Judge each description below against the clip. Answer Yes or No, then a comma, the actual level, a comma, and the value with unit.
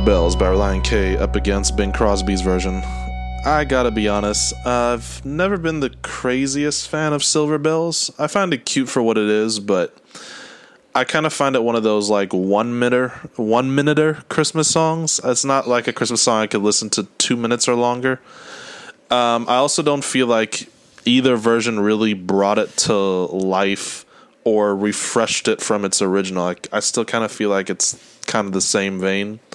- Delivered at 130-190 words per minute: Yes, average, 185 wpm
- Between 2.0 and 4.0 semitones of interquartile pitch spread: No, average, 5.1 semitones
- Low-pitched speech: Yes, low, 120 Hz